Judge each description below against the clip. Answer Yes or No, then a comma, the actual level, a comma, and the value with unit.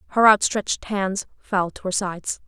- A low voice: No, high, 195 Hz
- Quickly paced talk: No, average, 170 wpm